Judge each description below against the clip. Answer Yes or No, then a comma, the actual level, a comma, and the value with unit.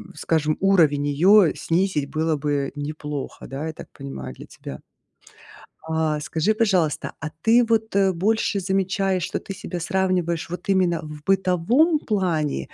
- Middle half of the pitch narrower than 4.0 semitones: No, average, 4.3 semitones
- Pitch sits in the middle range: Yes, medium, 170 Hz